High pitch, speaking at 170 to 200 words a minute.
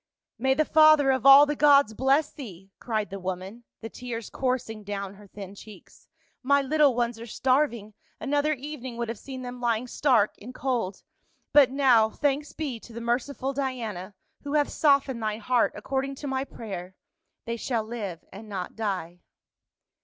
Yes: high, 245 Hz; average, 175 wpm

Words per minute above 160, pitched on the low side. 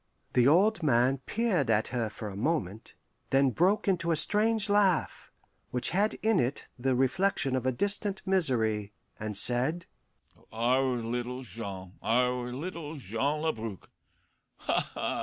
No: average, 140 wpm; low, 130 Hz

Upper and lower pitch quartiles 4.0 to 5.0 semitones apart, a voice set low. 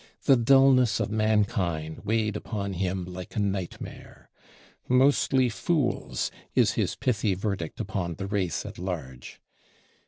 Yes: average, 4.5 semitones; low, 100 Hz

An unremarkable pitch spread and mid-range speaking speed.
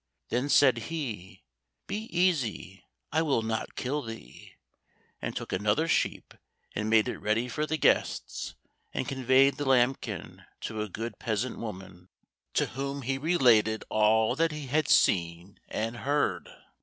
Yes: average, 4.9 semitones; average, 145 wpm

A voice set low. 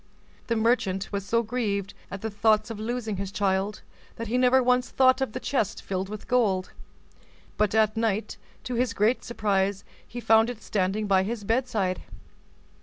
No: high, 215 Hz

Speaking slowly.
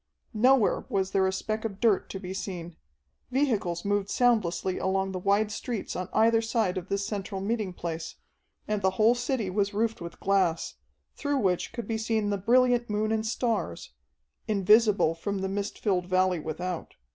No: average, 175 wpm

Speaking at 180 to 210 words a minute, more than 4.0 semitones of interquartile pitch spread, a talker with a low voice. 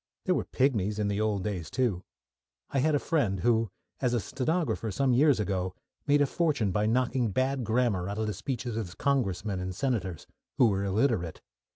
Yes: average, 190 wpm; average, 4.9 semitones; low, 110 Hz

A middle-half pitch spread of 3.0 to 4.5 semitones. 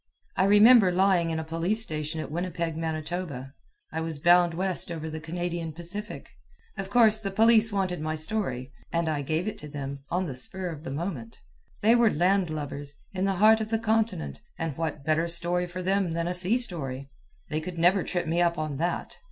Yes: average, 3.6 semitones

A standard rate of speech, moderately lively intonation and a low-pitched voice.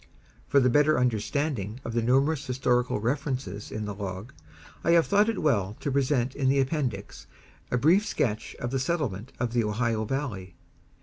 Yes: average, 175 wpm; average, 4.6 semitones; low, 125 Hz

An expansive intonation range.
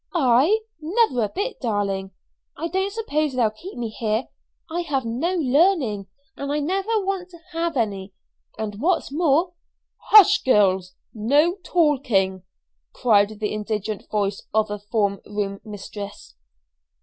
Yes: wide, 8.5 semitones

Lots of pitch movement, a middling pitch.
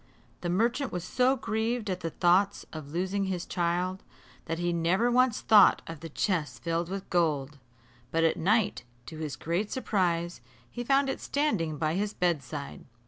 No: average, 4.4 semitones; medium, 180 Hz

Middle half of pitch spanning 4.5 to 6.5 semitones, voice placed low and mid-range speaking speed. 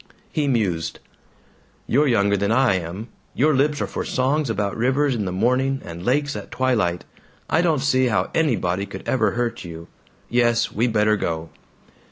Yes: average, 5.1 semitones; low, 120 Hz; average, 170 wpm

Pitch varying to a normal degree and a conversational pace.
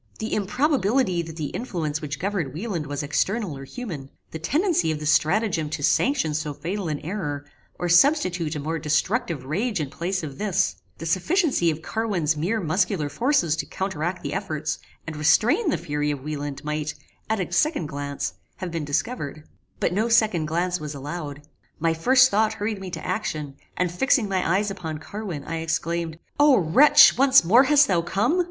No: wide, 6.0 semitones; average, 180 wpm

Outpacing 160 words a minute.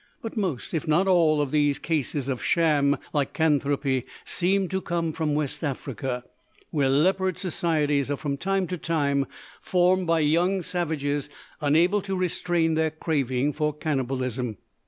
No: average, 145 wpm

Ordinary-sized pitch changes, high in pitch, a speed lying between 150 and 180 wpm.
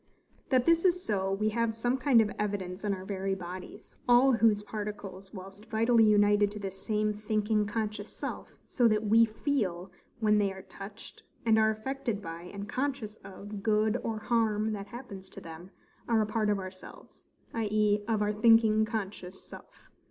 No: narrow, 2.2 semitones; high, 210 Hz; average, 175 wpm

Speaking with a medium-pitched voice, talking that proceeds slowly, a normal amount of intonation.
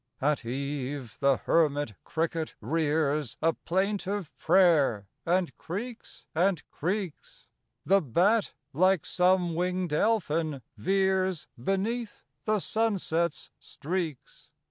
Yes: medium, 170 Hz; slow, 100 wpm; average, 4.4 semitones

